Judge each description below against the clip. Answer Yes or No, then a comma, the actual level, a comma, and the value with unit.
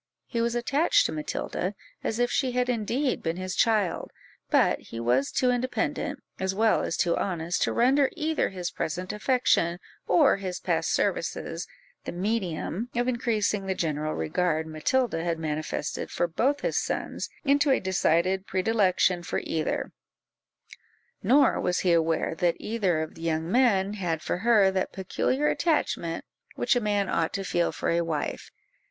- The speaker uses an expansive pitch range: Yes, wide, 6.0 semitones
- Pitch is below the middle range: No, high, 190 Hz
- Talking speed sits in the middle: Yes, average, 160 wpm